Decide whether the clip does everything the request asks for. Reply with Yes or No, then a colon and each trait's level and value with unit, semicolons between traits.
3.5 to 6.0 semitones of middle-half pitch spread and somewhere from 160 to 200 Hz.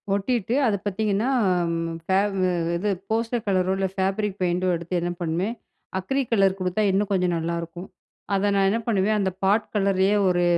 No: narrow, 2.6 semitones; high, 190 Hz